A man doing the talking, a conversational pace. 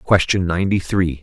Yes: male; average, 145 wpm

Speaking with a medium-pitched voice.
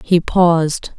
Yes: medium, 170 Hz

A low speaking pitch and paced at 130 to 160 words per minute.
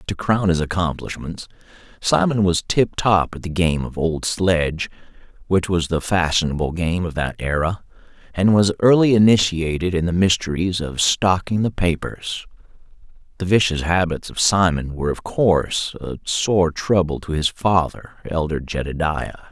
Yes: very low, 85 Hz; average, 150 wpm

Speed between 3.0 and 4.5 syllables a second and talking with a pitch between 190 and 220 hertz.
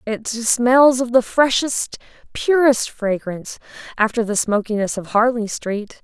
No: 4.1 syllables/s; high, 230 Hz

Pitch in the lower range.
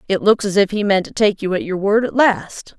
No: high, 200 Hz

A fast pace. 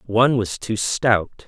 No: average, 160 wpm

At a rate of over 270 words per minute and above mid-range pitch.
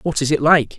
No: fast, 305 wpm; medium, 145 Hz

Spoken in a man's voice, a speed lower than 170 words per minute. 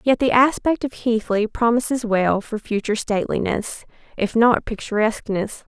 No: female; slow, 135 wpm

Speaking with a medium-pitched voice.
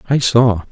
No: low, 115 Hz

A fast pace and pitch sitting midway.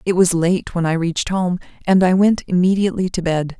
Yes: fast, 215 wpm; medium, 180 Hz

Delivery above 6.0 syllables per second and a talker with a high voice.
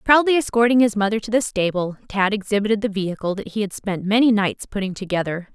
Yes: 6.2 syllables/s; high, 210 Hz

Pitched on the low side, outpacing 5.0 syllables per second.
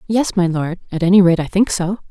No: medium, 185 Hz; 5.8 syllables/s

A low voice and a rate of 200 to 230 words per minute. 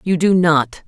No: medium, 165 Hz; fast, 205 wpm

